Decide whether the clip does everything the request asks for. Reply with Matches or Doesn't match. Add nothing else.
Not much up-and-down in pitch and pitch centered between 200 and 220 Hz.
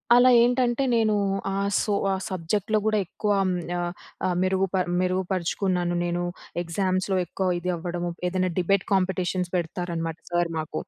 Doesn't match